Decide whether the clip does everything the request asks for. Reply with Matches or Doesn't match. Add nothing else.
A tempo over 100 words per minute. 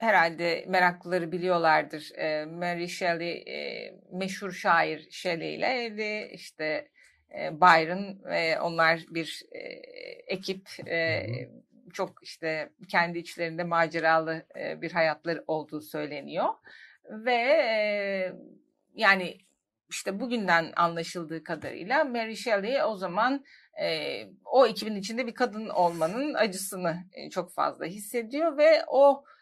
Doesn't match